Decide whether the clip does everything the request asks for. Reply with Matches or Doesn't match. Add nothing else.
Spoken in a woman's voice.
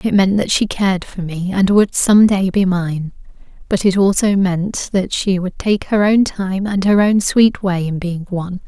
Matches